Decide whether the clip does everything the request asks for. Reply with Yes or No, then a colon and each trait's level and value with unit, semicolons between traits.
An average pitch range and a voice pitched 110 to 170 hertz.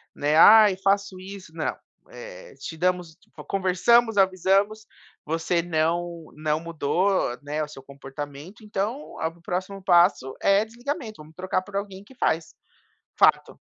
No: average, 4.0 semitones; medium, 185 Hz